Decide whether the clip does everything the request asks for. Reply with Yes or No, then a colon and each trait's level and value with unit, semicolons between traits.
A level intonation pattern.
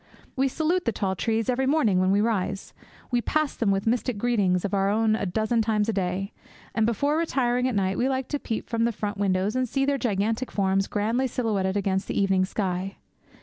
No: average, 4.0 semitones